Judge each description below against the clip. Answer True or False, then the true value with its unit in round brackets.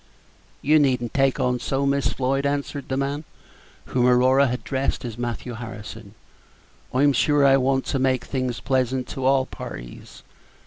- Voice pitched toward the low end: True (130 Hz)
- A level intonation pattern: True (1.8 semitones)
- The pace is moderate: True (165 wpm)